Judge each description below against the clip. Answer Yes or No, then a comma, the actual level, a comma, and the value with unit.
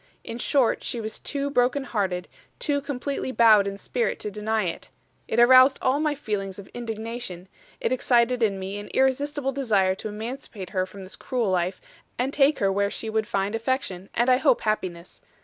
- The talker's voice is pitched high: Yes, high, 225 Hz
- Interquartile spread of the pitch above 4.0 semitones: Yes, average, 4.6 semitones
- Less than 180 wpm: No, average, 185 wpm